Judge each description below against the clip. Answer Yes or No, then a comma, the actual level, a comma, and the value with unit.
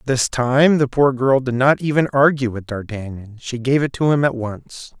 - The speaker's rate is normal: No, fast, 215 wpm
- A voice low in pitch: Yes, low, 125 Hz